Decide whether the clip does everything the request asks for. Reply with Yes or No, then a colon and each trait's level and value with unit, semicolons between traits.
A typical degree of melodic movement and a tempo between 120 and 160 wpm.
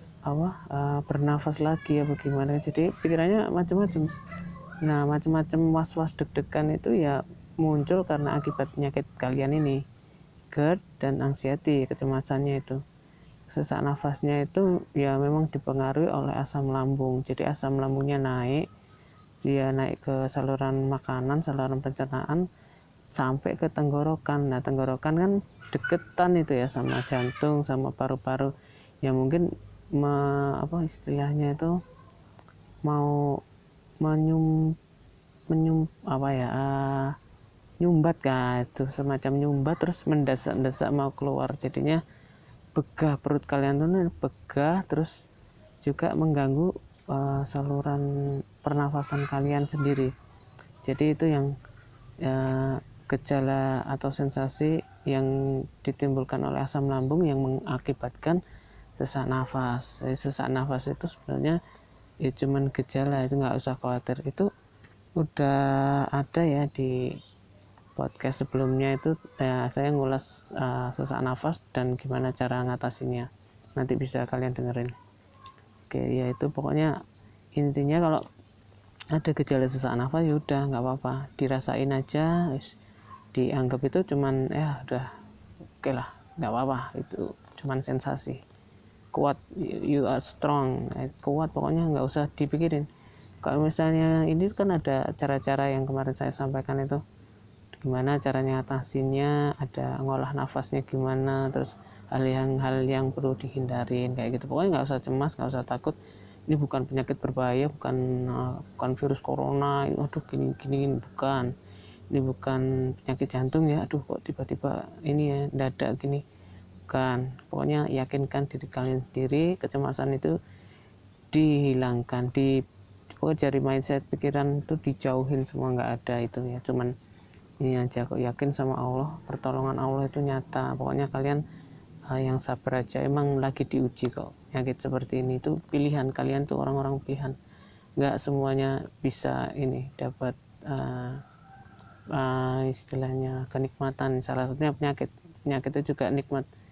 No: narrow, 2.1 semitones; average, 125 wpm